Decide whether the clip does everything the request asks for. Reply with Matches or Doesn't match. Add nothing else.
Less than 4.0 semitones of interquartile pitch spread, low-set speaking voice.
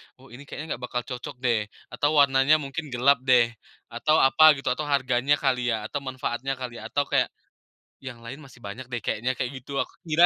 Matches